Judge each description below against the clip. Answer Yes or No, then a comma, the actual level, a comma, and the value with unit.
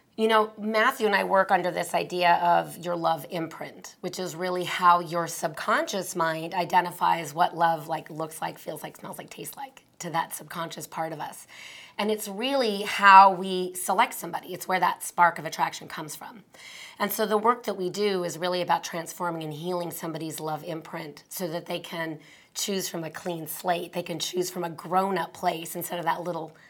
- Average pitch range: No, narrow, 2.3 semitones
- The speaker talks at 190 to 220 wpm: Yes, average, 200 wpm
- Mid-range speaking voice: Yes, medium, 175 Hz